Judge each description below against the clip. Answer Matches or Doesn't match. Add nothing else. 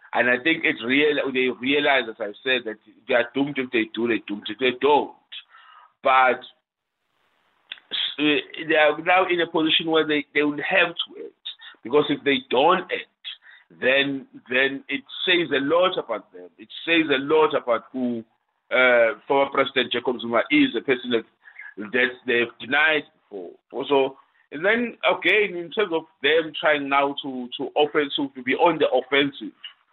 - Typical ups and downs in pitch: Matches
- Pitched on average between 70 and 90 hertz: Doesn't match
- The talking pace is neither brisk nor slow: Matches